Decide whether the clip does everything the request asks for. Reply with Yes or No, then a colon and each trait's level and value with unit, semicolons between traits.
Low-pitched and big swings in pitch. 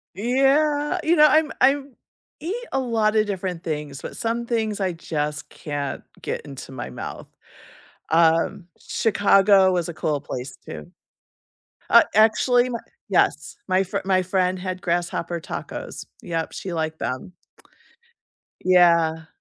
No: medium, 185 Hz; wide, 6.2 semitones